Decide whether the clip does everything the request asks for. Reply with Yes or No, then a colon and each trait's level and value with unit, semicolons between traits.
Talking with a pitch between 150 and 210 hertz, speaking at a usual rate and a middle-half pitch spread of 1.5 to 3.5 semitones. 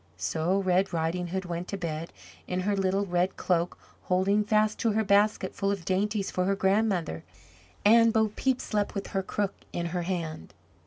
Yes: high, 190 Hz; average, 180 wpm; average, 2.8 semitones